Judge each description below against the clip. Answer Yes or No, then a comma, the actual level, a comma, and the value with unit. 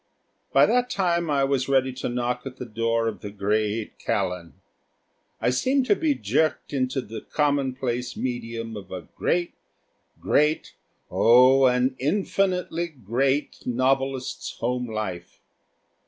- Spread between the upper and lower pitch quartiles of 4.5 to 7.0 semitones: No, average, 3.9 semitones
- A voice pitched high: No, low, 130 Hz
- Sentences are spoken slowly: Yes, slow, 130 wpm